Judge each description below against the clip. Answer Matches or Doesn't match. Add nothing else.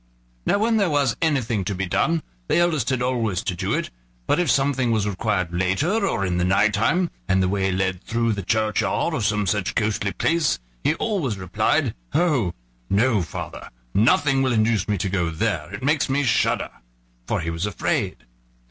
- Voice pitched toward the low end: Matches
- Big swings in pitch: Matches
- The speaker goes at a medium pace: Matches